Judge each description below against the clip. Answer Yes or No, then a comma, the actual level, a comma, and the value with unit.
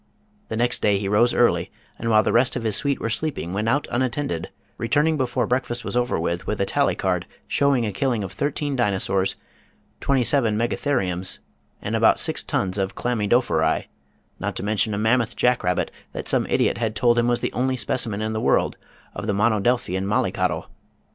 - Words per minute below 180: No, average, 190 wpm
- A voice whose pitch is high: No, low, 115 Hz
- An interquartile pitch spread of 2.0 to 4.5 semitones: Yes, average, 3.6 semitones